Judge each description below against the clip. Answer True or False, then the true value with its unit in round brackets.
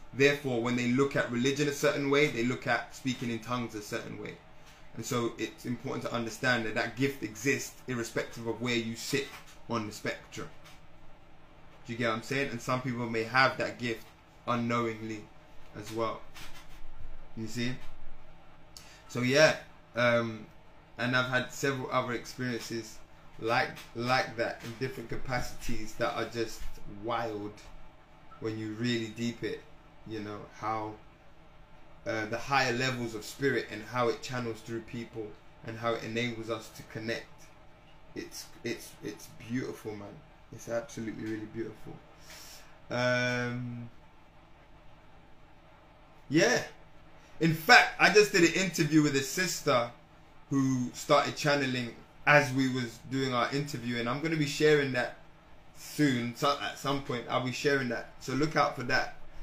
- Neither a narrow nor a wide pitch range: True (4.0 semitones)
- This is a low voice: True (125 Hz)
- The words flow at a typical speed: True (150 wpm)